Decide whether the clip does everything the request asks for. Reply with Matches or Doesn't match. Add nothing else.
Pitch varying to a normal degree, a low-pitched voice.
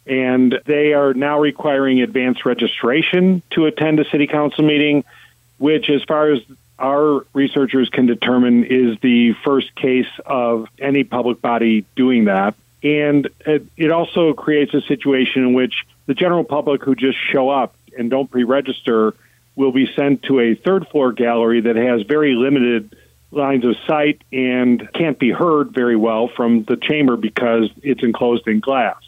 Matches